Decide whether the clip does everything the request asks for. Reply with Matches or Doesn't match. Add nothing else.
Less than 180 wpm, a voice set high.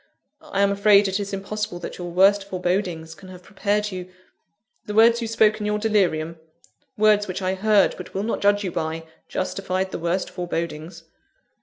Doesn't match